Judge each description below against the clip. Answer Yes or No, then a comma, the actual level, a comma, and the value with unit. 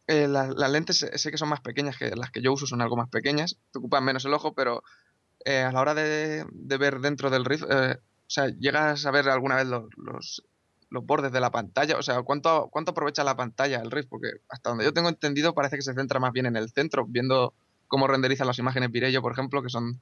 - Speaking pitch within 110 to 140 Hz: Yes, low, 135 Hz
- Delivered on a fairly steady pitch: Yes, narrow, 2.3 semitones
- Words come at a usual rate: No, fast, 250 wpm